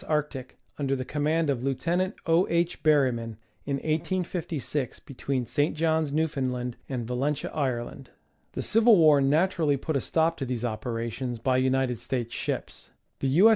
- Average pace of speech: Yes, average, 155 wpm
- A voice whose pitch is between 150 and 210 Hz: No, medium, 140 Hz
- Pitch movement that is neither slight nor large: Yes, average, 3.9 semitones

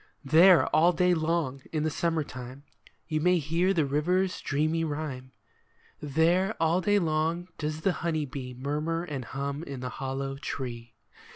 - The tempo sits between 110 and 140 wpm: No, average, 160 wpm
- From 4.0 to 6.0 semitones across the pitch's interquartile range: No, average, 3.5 semitones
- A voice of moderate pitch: Yes, medium, 155 Hz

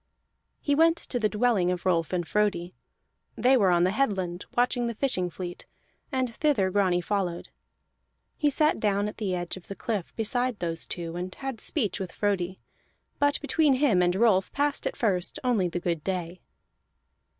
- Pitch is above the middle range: Yes, high, 200 Hz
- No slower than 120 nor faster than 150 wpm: No, average, 180 wpm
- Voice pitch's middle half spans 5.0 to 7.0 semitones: Yes, wide, 5.6 semitones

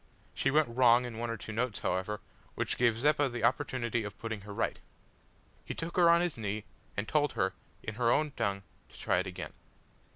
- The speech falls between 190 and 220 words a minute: Yes, fast, 205 wpm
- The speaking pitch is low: Yes, low, 115 Hz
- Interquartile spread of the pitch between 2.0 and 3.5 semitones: No, average, 4.5 semitones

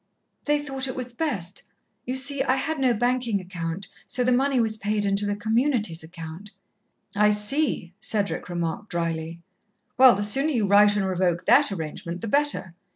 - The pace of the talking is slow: No, average, 170 wpm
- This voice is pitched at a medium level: No, high, 210 Hz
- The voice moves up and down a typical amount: No, wide, 6.0 semitones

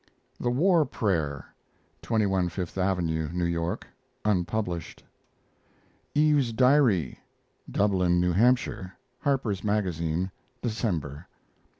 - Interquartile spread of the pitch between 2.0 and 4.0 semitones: No, average, 5.3 semitones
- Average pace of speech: No, slow, 85 wpm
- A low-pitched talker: Yes, very low, 95 Hz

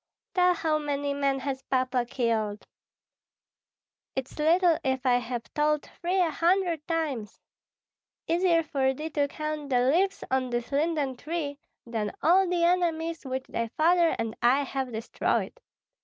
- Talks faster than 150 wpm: No, average, 145 wpm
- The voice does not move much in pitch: No, average, 4.4 semitones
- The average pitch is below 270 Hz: No, very high, 285 Hz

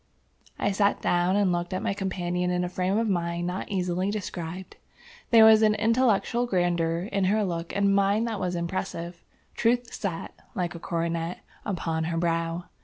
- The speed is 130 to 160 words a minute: No, average, 175 wpm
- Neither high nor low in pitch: Yes, medium, 180 Hz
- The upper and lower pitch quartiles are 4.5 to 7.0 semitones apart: No, average, 2.9 semitones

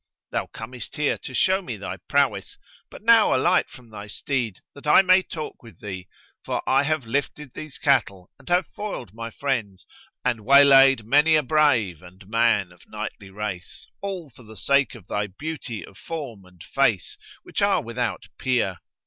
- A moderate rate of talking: Yes, average, 175 wpm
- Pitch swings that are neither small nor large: No, wide, 6.2 semitones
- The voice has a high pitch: No, low, 125 Hz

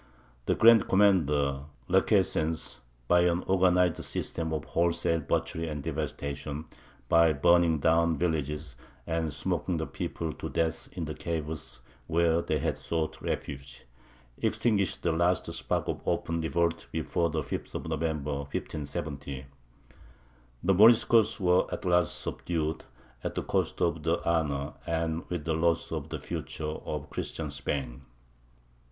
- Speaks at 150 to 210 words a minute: No, slow, 135 wpm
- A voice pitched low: Yes, very low, 80 Hz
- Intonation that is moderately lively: No, narrow, 2.2 semitones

